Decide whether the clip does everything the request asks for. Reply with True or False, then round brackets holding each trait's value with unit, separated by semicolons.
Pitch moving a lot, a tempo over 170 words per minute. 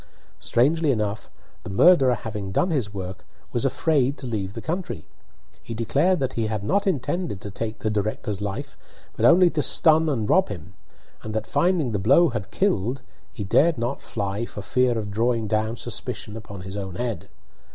True (5.9 semitones; 185 wpm)